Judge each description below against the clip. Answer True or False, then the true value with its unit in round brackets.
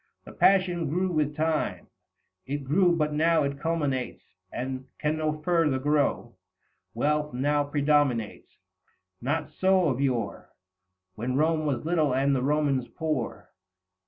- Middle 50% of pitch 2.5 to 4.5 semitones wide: True (3.0 semitones)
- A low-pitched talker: False (150 Hz)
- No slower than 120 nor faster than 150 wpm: True (135 wpm)